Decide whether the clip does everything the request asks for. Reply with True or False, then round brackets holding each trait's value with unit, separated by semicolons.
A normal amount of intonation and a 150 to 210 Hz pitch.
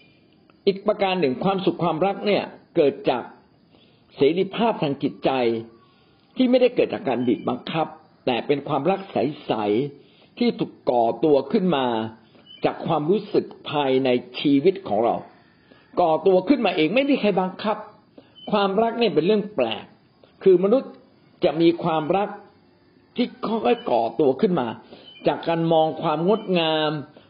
False (5.8 semitones; 185 Hz)